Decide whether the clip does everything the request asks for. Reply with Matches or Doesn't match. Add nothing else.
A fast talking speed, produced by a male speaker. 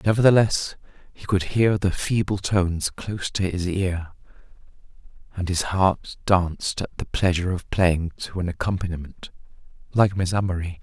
Doesn't match